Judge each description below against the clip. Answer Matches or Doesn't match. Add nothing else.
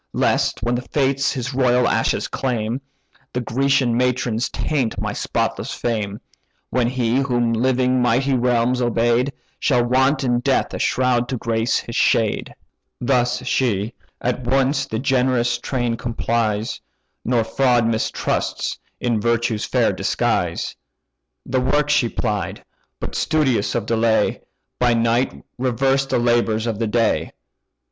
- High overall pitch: Doesn't match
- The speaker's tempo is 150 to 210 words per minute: Doesn't match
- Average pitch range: Doesn't match